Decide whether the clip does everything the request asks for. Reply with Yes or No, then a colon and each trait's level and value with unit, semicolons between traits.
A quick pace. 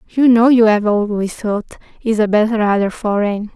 No: slow, 135 wpm